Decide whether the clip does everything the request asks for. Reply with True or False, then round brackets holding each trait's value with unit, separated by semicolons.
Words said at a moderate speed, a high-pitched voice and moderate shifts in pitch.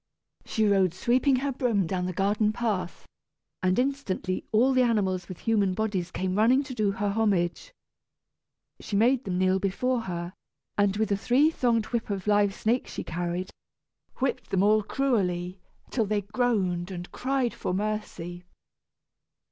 True (155 wpm; 205 Hz; 4.3 semitones)